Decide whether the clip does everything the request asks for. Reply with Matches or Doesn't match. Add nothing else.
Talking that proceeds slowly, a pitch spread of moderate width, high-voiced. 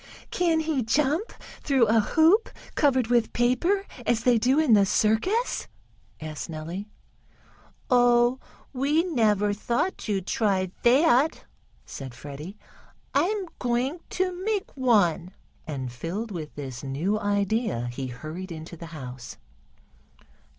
Doesn't match